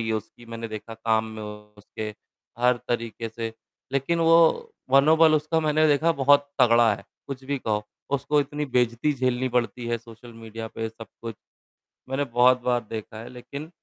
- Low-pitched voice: Yes, low, 120 Hz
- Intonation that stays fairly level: No, average, 3.8 semitones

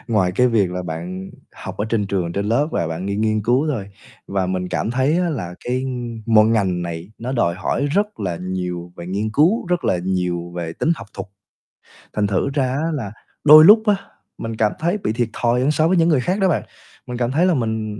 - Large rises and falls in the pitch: Yes, wide, 7.4 semitones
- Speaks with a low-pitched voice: Yes, low, 110 Hz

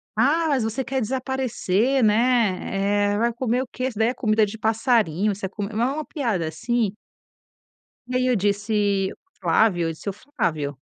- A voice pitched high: Yes, high, 220 Hz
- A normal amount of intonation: Yes, average, 4.1 semitones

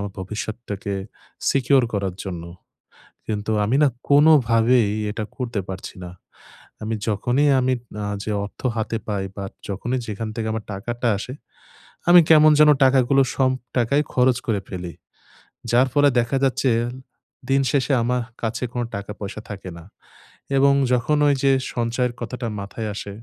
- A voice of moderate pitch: No, low, 120 Hz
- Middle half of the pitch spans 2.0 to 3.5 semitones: No, average, 3.9 semitones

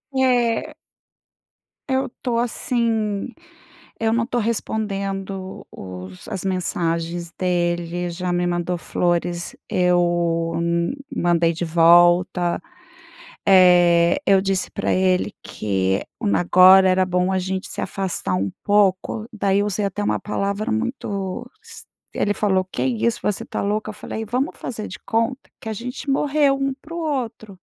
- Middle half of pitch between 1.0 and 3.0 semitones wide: No, average, 4.3 semitones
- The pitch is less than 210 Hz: Yes, high, 190 Hz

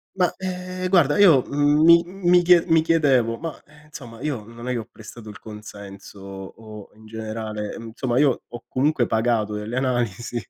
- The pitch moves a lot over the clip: Yes, wide, 6.3 semitones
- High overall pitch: No, low, 120 Hz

